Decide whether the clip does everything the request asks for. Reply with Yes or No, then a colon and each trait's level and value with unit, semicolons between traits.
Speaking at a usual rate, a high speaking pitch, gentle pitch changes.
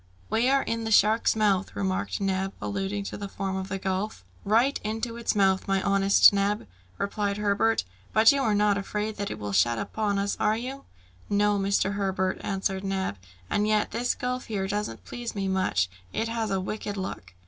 Yes: average, 190 wpm; high, 200 Hz; narrow, 2.1 semitones